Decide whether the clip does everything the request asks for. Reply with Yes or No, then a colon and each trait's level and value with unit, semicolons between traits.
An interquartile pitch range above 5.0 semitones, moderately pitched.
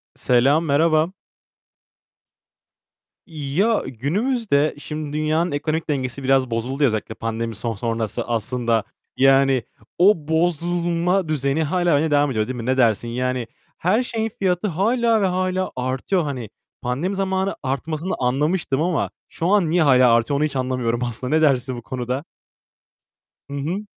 Yes: wide, 5.5 semitones; medium, 145 Hz